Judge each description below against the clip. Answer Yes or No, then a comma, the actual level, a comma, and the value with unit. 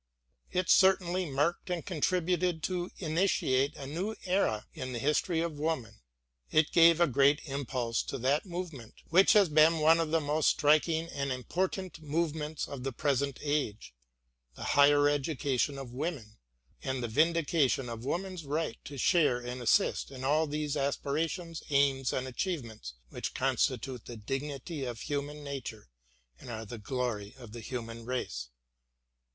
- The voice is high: No, medium, 145 Hz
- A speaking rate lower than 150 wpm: No, average, 155 wpm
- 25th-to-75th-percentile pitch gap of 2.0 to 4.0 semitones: No, average, 4.5 semitones